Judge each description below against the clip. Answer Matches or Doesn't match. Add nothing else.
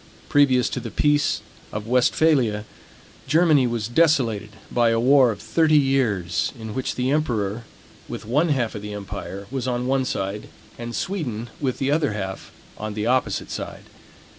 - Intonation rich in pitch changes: Doesn't match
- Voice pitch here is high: Doesn't match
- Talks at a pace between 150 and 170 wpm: Matches